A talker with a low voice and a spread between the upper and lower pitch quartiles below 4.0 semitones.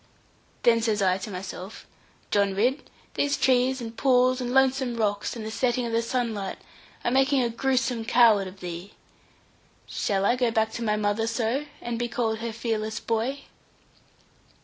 No: high, 230 Hz; average, 2.8 semitones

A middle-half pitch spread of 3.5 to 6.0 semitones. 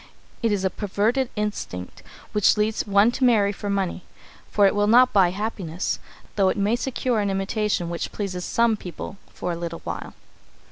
No: narrow, 2.6 semitones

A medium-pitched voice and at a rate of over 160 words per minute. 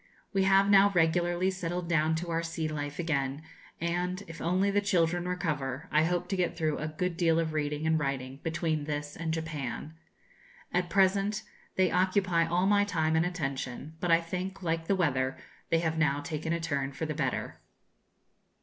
Yes: medium, 165 Hz; average, 185 wpm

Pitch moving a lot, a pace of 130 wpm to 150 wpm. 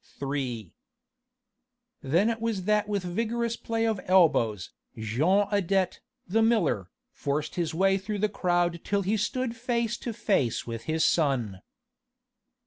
Yes: wide, 6.9 semitones; average, 140 wpm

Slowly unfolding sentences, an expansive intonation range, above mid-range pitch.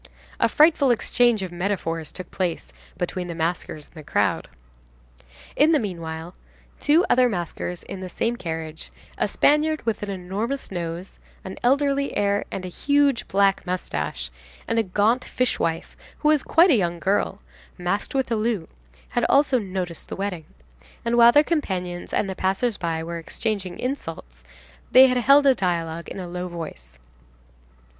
No: average, 160 wpm; wide, 6.1 semitones; high, 195 Hz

